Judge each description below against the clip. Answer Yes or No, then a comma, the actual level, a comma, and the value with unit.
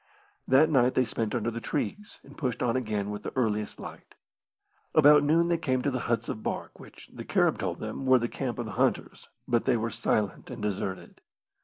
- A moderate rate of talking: No, fast, 210 wpm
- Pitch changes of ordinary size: Yes, average, 3.8 semitones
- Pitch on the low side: Yes, low, 120 Hz